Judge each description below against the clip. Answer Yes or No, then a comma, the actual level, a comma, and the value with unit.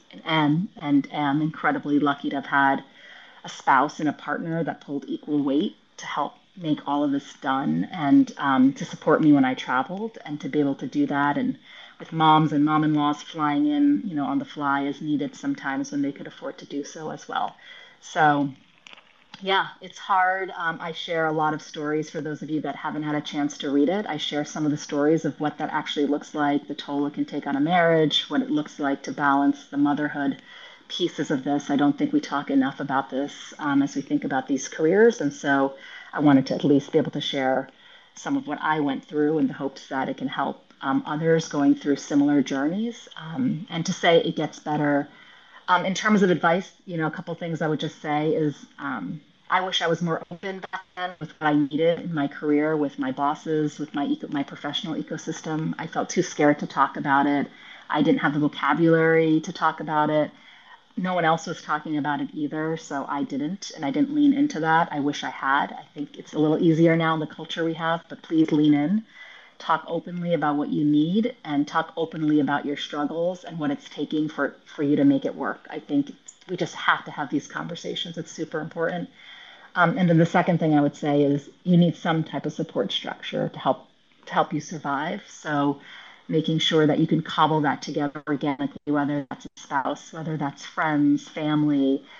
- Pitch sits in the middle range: Yes, medium, 155 Hz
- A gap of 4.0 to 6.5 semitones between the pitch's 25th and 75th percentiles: No, average, 3.5 semitones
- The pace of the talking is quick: Yes, fast, 220 wpm